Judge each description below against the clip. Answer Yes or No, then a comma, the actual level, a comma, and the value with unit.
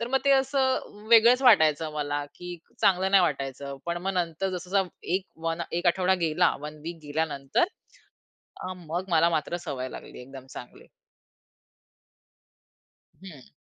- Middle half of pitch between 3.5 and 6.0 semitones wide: Yes, average, 4.5 semitones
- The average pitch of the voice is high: No, medium, 170 Hz